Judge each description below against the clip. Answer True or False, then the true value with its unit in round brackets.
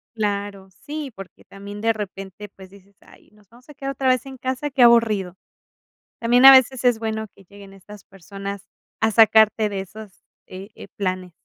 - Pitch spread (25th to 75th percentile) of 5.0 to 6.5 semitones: False (3.4 semitones)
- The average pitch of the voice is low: False (210 Hz)